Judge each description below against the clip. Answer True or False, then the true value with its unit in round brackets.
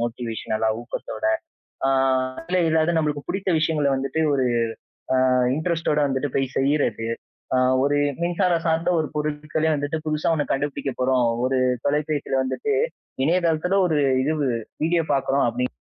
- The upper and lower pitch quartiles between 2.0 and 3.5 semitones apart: True (3.2 semitones)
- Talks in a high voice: False (150 Hz)